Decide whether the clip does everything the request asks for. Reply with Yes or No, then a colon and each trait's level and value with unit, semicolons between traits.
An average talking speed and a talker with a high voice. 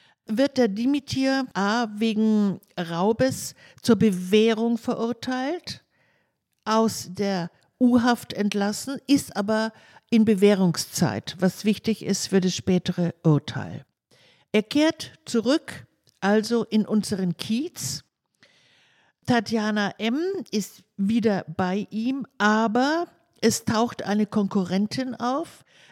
No: slow, 100 wpm; high, 215 Hz